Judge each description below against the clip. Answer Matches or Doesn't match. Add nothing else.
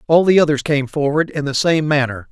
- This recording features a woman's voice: Doesn't match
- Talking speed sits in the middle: Doesn't match